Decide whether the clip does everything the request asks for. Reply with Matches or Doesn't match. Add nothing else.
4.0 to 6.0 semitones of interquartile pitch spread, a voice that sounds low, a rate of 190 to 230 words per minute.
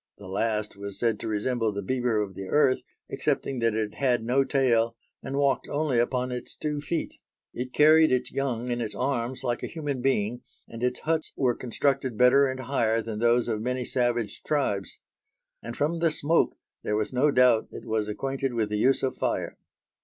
Doesn't match